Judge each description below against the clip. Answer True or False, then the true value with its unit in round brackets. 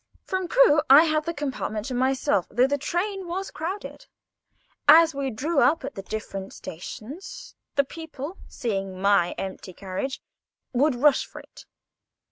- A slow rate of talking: False (150 wpm)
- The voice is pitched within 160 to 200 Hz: False (275 Hz)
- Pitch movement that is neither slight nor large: False (7.2 semitones)